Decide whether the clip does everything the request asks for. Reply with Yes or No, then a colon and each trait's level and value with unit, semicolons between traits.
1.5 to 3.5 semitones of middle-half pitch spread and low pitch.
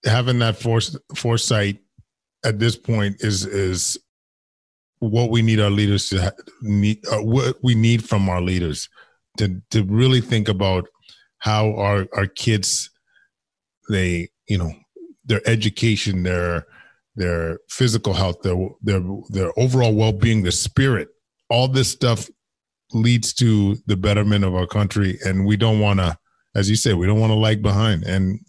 Yes: average, 2.9 semitones; low, 105 Hz